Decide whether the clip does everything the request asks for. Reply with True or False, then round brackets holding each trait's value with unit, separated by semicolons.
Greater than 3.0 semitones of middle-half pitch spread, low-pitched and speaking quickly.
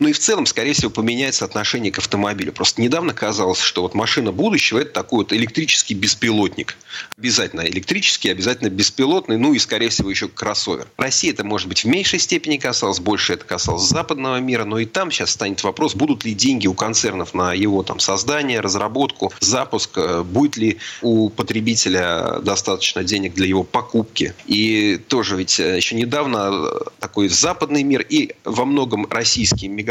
True (4.6 semitones; 115 Hz; 170 wpm)